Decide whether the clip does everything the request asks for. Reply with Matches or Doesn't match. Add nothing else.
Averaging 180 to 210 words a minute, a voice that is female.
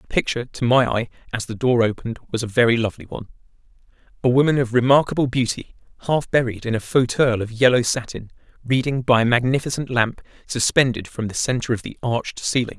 Doesn't match